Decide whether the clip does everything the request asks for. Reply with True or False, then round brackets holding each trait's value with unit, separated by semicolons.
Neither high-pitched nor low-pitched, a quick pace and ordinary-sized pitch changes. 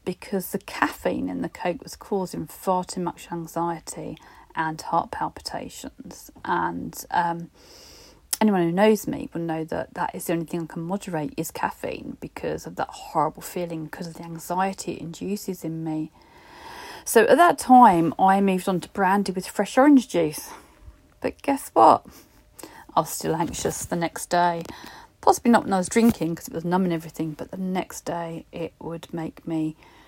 False (180 Hz; 180 wpm; 3.6 semitones)